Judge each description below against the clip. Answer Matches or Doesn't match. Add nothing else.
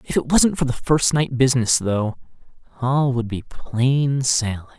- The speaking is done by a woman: Doesn't match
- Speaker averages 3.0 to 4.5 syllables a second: Matches